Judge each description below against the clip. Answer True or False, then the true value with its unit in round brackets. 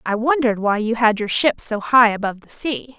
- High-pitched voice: True (230 Hz)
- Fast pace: True (240 wpm)